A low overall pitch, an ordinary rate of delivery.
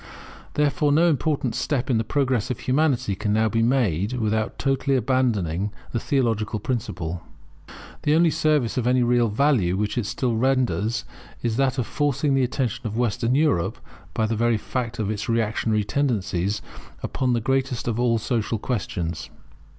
Yes: low, 120 Hz; average, 165 wpm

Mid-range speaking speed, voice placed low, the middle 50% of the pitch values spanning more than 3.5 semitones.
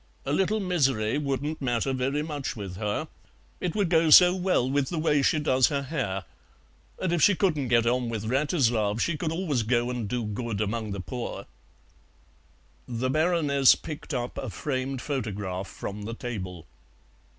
Yes: average, 170 wpm; low, 130 Hz; average, 5.1 semitones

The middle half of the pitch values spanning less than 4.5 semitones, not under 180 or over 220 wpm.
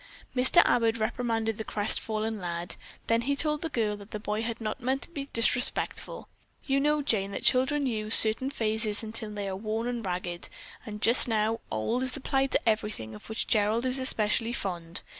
Yes: average, 3.2 semitones; average, 185 wpm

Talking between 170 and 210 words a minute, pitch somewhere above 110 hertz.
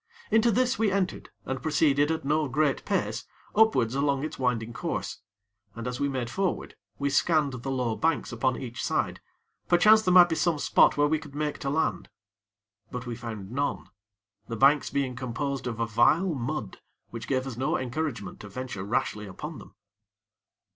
Yes: average, 180 wpm; low, 135 Hz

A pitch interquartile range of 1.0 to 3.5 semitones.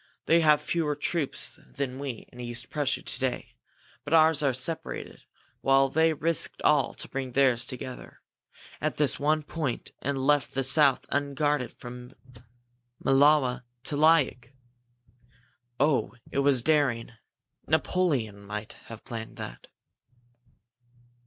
Yes: average, 3.2 semitones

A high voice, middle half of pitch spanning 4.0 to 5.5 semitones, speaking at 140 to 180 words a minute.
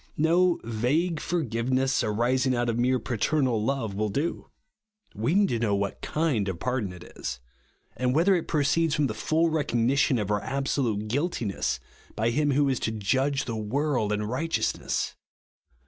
No: low, 130 Hz; average, 5.2 semitones; average, 165 wpm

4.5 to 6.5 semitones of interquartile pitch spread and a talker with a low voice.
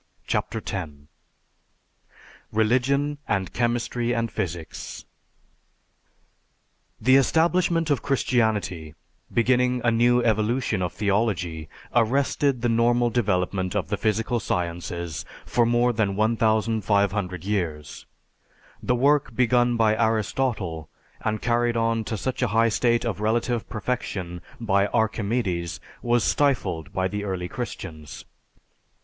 No: average, 3.8 semitones; low, 110 Hz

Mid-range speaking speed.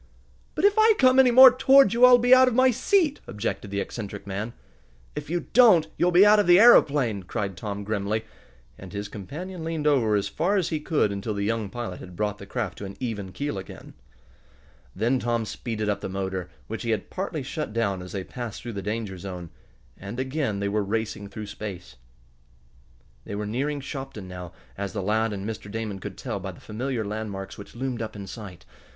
No: fast, 210 wpm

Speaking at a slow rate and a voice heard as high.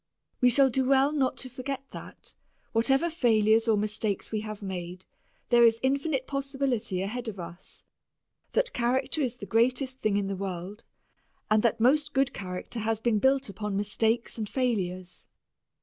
No: average, 165 wpm; high, 230 Hz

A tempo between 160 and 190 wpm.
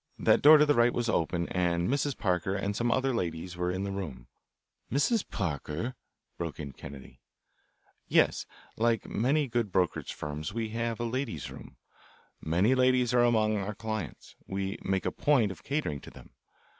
Yes: average, 180 wpm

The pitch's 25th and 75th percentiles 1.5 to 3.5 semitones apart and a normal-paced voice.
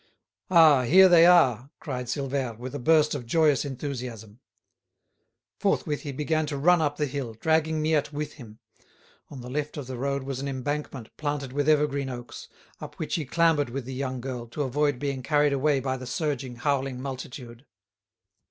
Yes: average, 2.8 semitones; average, 180 wpm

